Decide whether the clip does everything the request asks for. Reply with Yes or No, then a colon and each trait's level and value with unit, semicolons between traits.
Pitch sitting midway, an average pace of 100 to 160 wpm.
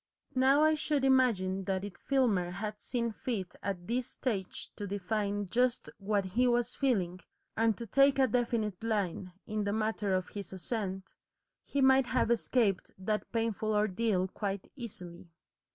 No: high, 215 Hz; average, 155 wpm